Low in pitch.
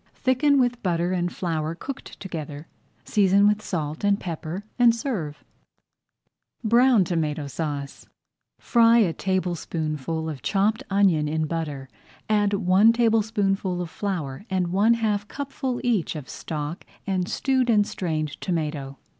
No: medium, 185 Hz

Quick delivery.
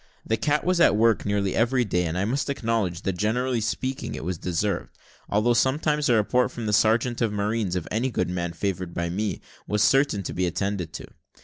Yes: fast, 210 wpm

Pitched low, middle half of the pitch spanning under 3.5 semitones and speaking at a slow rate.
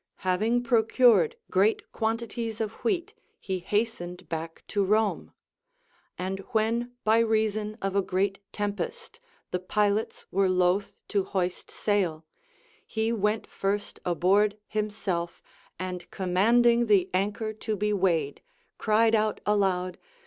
No: high, 205 Hz; average, 3.0 semitones; slow, 120 wpm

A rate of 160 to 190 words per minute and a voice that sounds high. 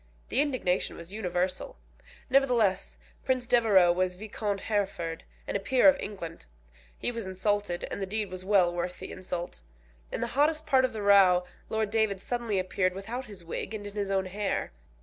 Yes: average, 180 wpm; high, 200 Hz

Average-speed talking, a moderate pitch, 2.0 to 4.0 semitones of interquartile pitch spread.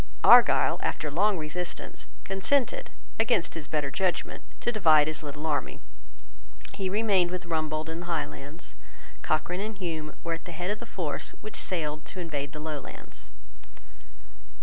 Yes: average, 150 wpm; medium, 165 Hz; average, 3.6 semitones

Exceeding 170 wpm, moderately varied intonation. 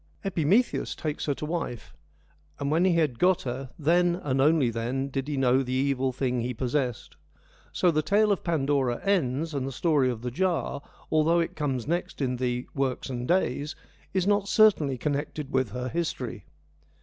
Yes: average, 185 wpm; average, 4.8 semitones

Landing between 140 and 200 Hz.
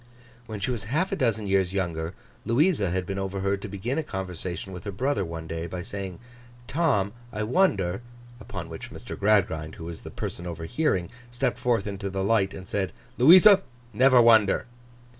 No: low, 100 Hz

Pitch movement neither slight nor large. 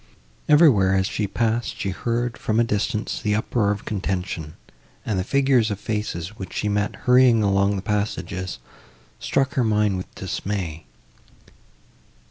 Yes: average, 3.2 semitones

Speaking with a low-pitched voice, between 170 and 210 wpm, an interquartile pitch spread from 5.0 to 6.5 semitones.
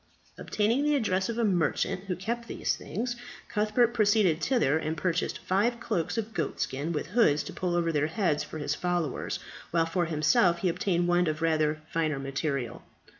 No: medium, 175 Hz; average, 180 wpm; average, 5.3 semitones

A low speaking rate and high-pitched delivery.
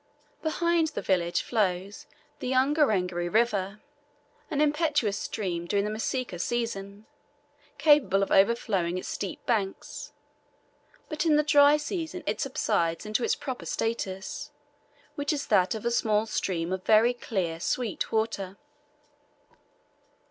Yes: slow, 125 wpm; high, 220 Hz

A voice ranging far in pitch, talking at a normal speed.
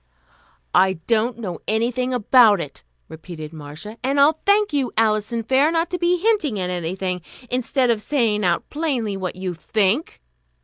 Yes: wide, 6.6 semitones; average, 160 wpm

